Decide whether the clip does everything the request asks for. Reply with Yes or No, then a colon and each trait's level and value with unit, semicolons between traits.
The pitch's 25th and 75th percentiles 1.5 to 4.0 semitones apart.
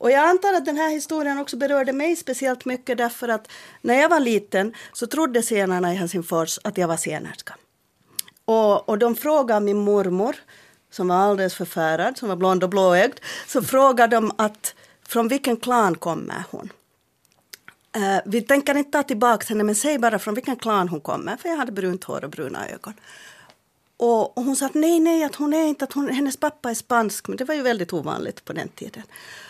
No: wide, 5.5 semitones